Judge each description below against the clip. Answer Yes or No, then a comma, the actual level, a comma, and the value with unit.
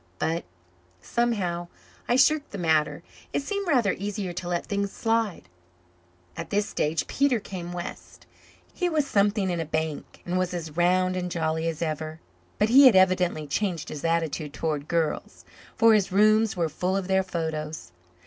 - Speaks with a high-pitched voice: No, medium, 180 Hz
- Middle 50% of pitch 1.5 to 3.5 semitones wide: No, average, 4.3 semitones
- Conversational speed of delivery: Yes, average, 170 wpm